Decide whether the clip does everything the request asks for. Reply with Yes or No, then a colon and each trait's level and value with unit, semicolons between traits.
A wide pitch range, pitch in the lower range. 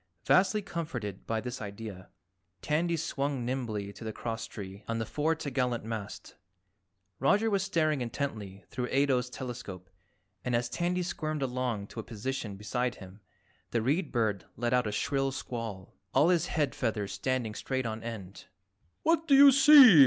Yes: wide, 5.7 semitones; low, 125 Hz